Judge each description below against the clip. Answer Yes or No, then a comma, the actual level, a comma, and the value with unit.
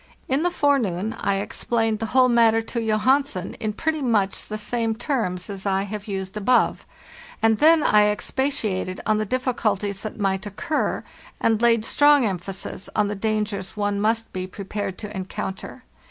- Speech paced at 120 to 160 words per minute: No, average, 170 wpm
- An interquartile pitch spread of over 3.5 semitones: No, average, 3.2 semitones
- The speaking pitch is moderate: No, high, 215 Hz